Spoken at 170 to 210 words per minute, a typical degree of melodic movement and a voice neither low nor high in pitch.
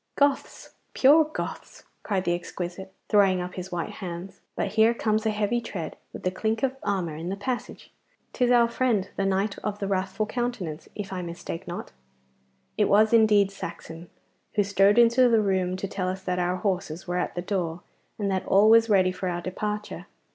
No: average, 190 wpm; average, 3.1 semitones; high, 195 Hz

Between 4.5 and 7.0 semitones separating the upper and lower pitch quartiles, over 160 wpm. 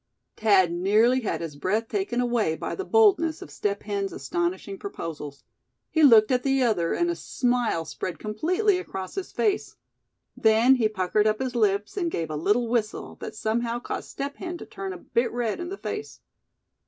Yes: wide, 5.6 semitones; average, 185 wpm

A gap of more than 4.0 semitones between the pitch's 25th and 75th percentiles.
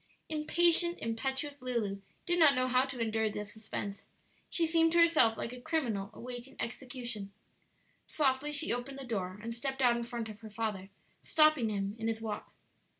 Yes: average, 4.4 semitones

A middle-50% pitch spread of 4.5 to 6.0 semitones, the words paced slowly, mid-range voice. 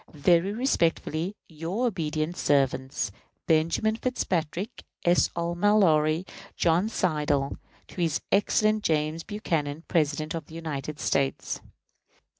No: average, 3.6 semitones; slow, 95 wpm; medium, 165 Hz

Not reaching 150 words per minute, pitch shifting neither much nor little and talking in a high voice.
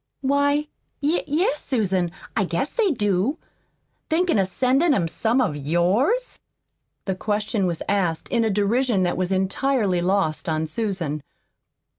No: average, 140 wpm; wide, 7.1 semitones; high, 205 Hz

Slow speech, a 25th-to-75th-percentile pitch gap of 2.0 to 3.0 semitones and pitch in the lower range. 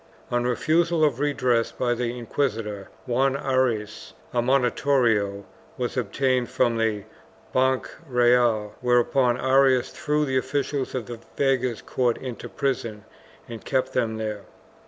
Yes: slow, 130 wpm; narrow, 2.5 semitones; low, 125 Hz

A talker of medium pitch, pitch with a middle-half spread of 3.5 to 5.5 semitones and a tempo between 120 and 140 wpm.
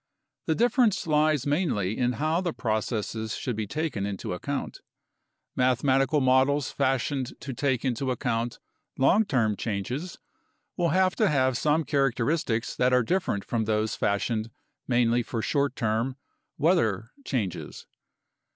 No: low, 130 Hz; average, 4.9 semitones; slow, 135 wpm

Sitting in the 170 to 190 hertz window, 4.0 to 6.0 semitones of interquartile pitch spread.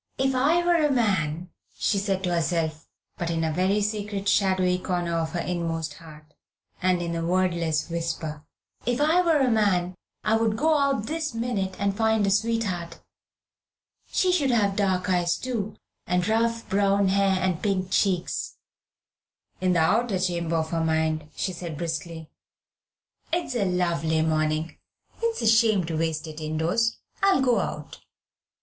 Yes: medium, 185 Hz; average, 5.0 semitones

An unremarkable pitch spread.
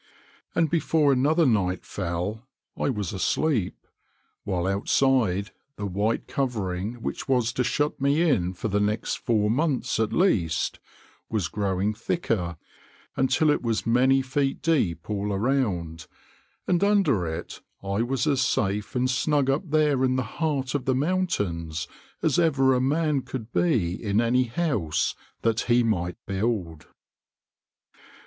No: wide, 5.8 semitones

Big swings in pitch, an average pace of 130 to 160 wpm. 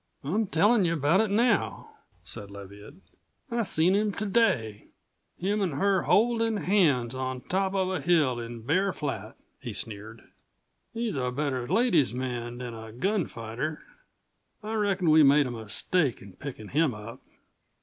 Yes: wide, 8.3 semitones; average, 155 wpm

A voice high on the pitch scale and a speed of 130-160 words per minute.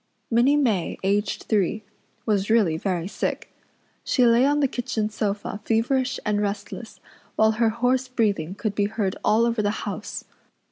Yes: high, 220 Hz; average, 155 wpm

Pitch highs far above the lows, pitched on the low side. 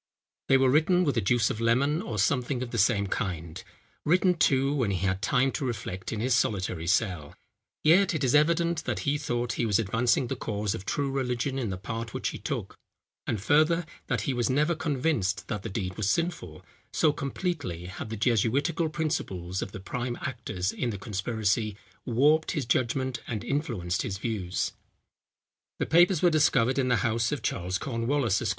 Yes: wide, 6.0 semitones; low, 120 Hz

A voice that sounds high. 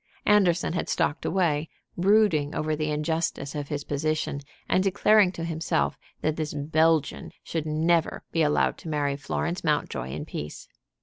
No: medium, 155 Hz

